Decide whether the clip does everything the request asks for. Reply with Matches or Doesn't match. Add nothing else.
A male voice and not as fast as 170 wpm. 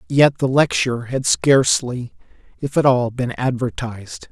Matches